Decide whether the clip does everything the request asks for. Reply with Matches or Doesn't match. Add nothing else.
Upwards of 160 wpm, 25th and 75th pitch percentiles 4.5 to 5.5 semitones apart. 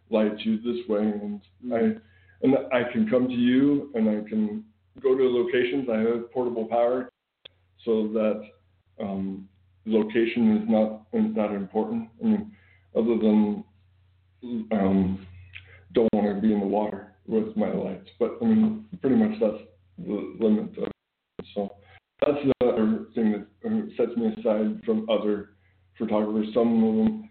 Doesn't match